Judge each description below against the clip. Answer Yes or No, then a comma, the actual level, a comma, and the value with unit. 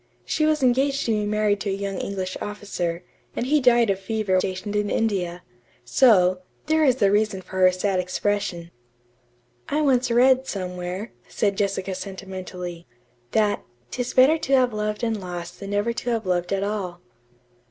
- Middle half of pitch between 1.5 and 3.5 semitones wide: No, average, 4.1 semitones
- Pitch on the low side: No, high, 205 Hz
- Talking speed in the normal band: Yes, average, 170 wpm